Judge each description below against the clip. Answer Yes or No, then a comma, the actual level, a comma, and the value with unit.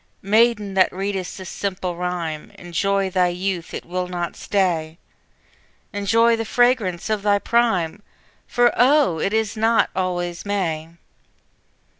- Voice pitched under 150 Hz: No, high, 195 Hz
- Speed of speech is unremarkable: No, slow, 130 wpm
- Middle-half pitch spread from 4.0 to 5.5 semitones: No, average, 3.4 semitones